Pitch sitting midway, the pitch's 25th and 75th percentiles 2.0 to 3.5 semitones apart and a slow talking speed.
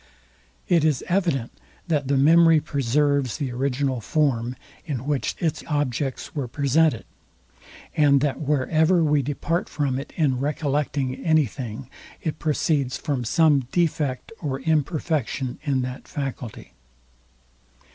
Yes: medium, 145 Hz; average, 3.0 semitones; slow, 125 wpm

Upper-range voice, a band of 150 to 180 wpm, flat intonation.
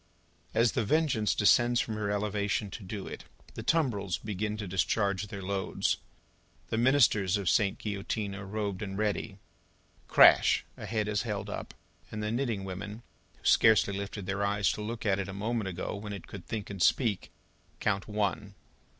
No: low, 105 Hz; average, 175 wpm; narrow, 1.7 semitones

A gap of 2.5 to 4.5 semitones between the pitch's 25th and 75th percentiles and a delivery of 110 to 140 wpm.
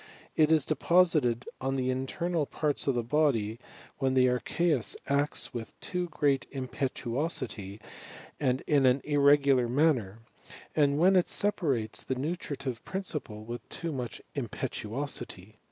Yes: average, 4.0 semitones; slow, 135 wpm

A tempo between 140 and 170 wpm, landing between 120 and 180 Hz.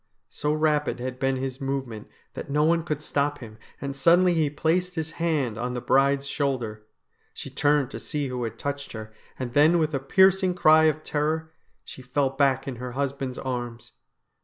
No: average, 185 wpm; medium, 140 Hz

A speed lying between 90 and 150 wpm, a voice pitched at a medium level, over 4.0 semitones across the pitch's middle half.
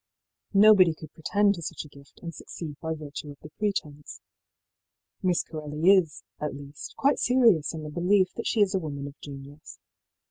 No: average, 180 wpm; medium, 160 Hz; average, 4.5 semitones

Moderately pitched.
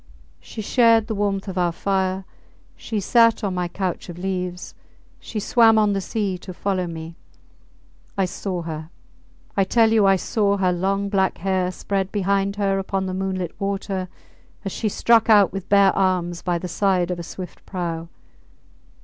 No: high, 195 Hz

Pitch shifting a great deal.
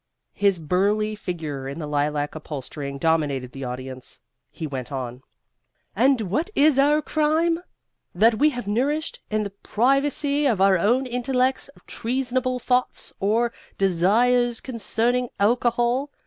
Yes: wide, 8.0 semitones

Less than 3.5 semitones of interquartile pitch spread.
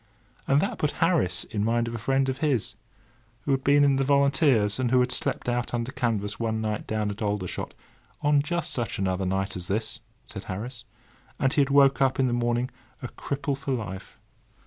No: average, 4.3 semitones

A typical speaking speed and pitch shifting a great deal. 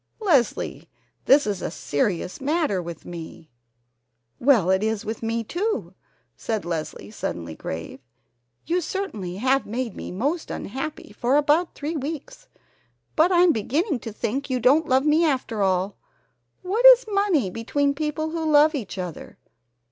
Yes: average, 150 wpm; wide, 8.3 semitones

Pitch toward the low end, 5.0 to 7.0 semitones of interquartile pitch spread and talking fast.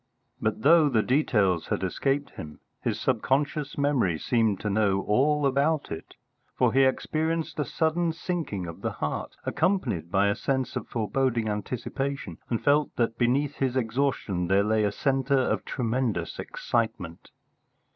No: low, 125 Hz; average, 5.3 semitones; average, 150 wpm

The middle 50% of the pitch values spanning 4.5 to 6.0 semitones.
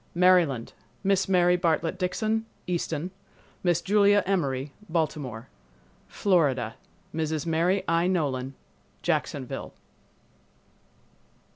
No: average, 4.1 semitones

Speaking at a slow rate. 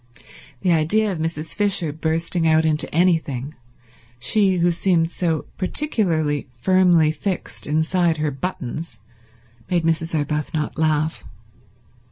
Yes: slow, 115 wpm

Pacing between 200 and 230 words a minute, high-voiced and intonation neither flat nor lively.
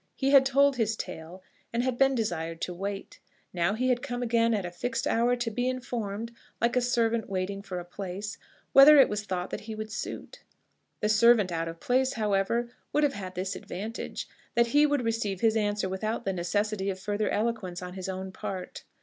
Yes: fast, 205 wpm; high, 215 Hz; average, 4.1 semitones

